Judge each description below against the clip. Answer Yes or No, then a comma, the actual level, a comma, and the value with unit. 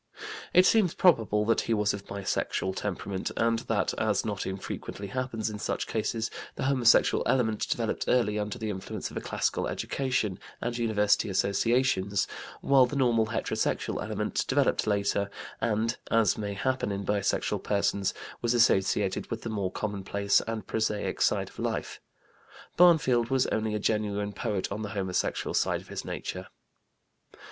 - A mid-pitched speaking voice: No, low, 110 Hz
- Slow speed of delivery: No, average, 155 wpm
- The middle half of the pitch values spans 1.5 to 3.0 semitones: Yes, narrow, 2.6 semitones